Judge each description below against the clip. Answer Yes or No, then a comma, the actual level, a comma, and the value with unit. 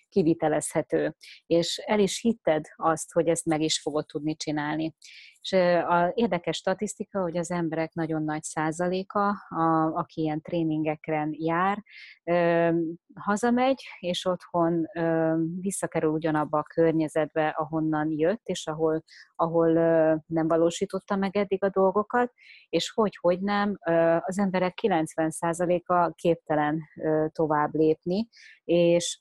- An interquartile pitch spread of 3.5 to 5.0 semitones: No, average, 2.7 semitones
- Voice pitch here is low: No, medium, 165 Hz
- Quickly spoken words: No, average, 120 wpm